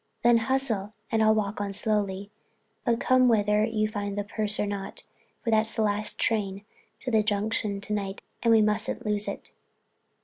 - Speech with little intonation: Yes, narrow, 1.6 semitones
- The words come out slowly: No, average, 180 wpm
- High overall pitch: Yes, high, 215 Hz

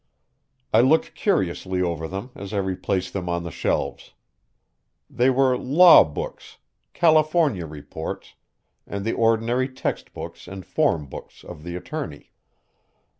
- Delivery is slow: Yes, slow, 130 wpm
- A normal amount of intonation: No, wide, 7.0 semitones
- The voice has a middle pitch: No, low, 100 Hz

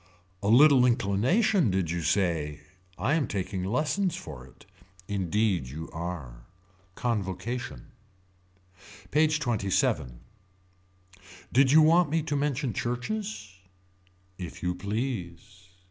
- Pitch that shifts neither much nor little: No, wide, 8.0 semitones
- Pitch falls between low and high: No, low, 110 Hz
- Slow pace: Yes, slow, 105 wpm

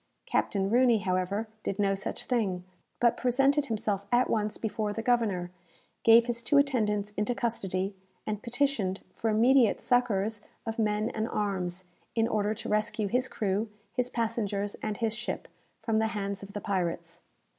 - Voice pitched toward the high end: Yes, high, 215 Hz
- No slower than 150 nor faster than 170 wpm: Yes, average, 160 wpm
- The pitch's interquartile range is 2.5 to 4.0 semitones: Yes, average, 2.8 semitones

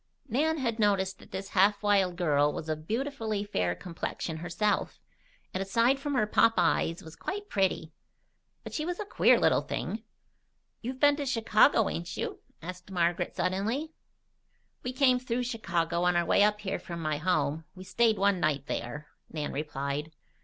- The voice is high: Yes, high, 195 Hz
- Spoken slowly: No, average, 170 wpm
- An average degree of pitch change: No, wide, 5.7 semitones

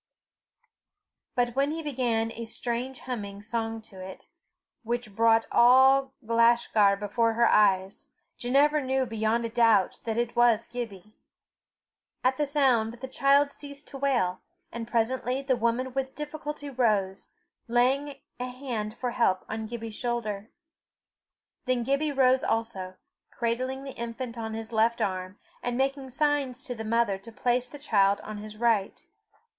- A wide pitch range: No, average, 3.0 semitones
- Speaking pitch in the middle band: No, high, 235 Hz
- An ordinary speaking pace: Yes, average, 150 wpm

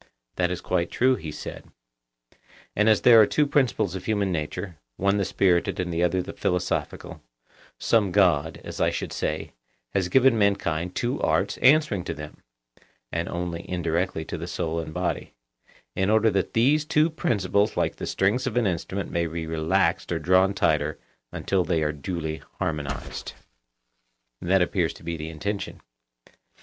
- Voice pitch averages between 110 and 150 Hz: No, very low, 90 Hz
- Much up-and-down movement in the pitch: No, average, 3.8 semitones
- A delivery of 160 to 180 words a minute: Yes, average, 165 wpm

